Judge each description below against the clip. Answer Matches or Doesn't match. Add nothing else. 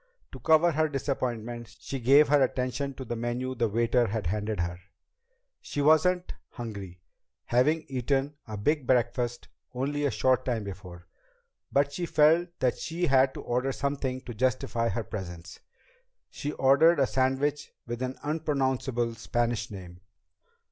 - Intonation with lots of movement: Doesn't match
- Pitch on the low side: Matches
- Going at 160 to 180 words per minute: Doesn't match